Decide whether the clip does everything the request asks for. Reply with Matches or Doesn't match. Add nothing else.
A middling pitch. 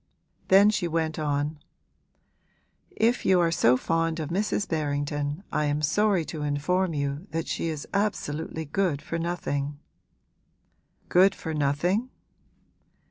Matches